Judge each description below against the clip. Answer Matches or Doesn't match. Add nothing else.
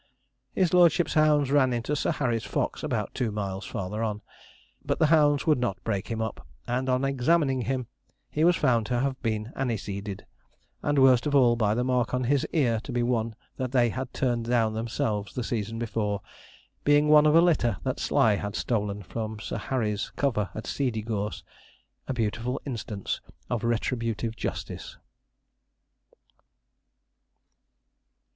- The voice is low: Matches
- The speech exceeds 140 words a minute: Matches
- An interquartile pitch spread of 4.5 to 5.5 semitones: Doesn't match